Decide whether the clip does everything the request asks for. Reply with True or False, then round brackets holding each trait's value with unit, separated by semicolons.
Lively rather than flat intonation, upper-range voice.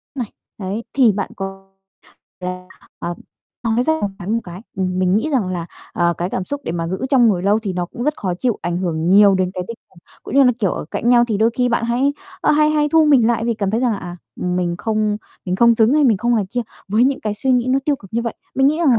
False (4.9 semitones; 220 Hz)